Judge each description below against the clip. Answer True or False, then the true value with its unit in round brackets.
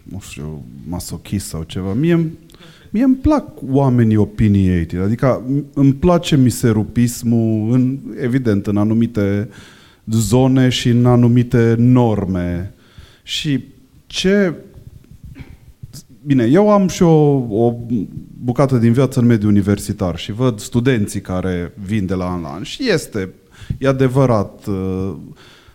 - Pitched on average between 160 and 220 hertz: False (120 Hz)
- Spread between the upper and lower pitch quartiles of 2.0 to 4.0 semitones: False (5.0 semitones)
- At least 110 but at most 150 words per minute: True (120 wpm)